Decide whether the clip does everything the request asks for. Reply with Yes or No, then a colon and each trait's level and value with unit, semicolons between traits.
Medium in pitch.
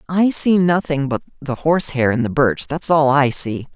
Yes: medium, 145 Hz